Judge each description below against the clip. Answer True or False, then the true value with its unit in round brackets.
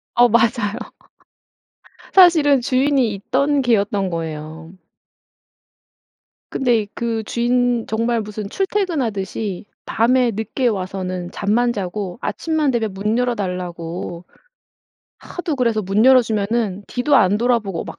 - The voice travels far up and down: False (4.0 semitones)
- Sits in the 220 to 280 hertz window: True (225 Hz)